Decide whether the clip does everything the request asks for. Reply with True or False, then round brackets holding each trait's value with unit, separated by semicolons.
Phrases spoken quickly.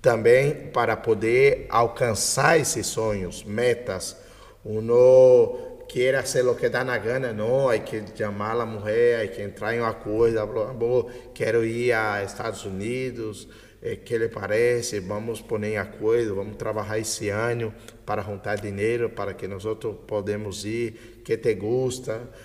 False (160 wpm)